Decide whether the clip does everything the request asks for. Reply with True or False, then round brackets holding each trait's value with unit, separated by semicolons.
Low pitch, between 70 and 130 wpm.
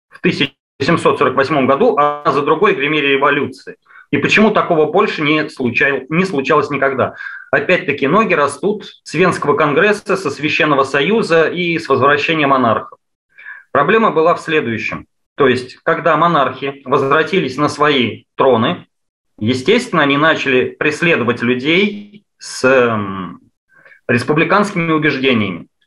False (150 Hz; 120 wpm)